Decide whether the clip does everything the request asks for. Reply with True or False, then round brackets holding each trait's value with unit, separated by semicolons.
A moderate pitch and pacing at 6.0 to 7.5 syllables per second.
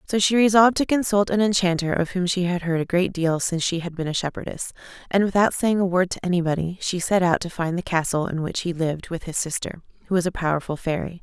True (180 Hz; 6.3 syllables/s)